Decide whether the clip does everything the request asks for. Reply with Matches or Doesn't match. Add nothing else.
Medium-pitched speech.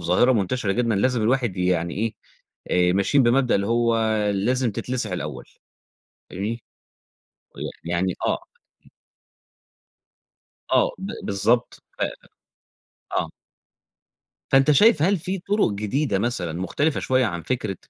Doesn't match